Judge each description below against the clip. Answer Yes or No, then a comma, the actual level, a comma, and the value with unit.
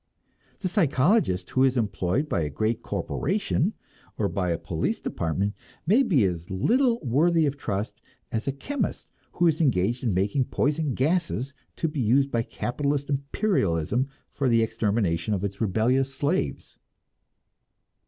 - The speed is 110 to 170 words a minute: Yes, average, 145 wpm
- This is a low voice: Yes, low, 125 Hz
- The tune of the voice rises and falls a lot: Yes, wide, 6.8 semitones